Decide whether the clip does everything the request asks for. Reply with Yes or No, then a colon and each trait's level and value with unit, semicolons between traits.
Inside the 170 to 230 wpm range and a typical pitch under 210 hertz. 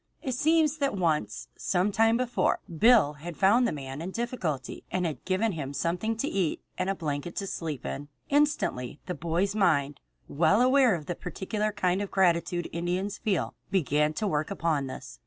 Yes: average, 180 wpm; medium, 185 Hz